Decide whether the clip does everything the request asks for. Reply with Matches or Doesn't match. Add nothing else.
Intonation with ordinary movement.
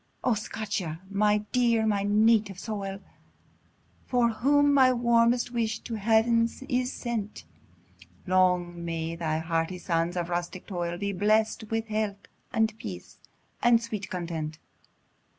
Matches